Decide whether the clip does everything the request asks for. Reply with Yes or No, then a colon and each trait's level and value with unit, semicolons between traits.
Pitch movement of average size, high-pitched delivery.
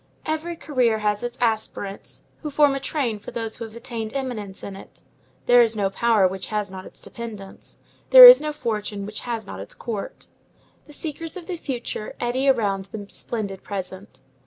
Yes: average, 4.7 semitones; high, 225 Hz